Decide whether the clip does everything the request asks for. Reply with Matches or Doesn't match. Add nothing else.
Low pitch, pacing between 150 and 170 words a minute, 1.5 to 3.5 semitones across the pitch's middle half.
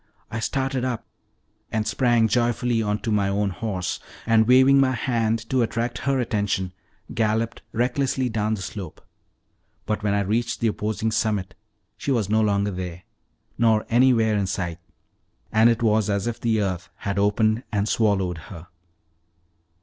Matches